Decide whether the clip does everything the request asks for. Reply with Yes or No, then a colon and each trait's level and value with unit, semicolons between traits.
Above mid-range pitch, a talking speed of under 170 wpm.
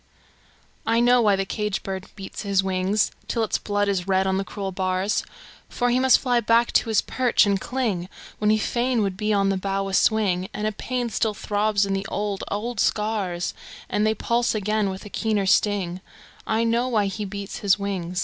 No: high, 205 Hz; fast, 205 wpm